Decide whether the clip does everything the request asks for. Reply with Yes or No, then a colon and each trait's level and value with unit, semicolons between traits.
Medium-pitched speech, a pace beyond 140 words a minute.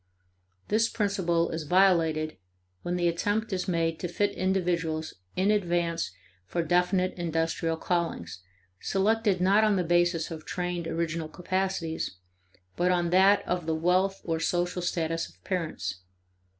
No: medium, 175 Hz; slow, 135 wpm